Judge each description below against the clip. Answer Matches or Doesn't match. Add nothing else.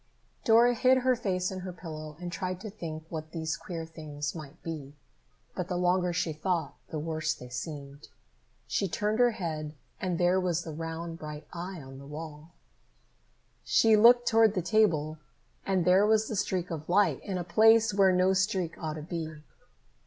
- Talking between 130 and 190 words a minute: Matches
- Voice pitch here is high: Doesn't match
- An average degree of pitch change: Matches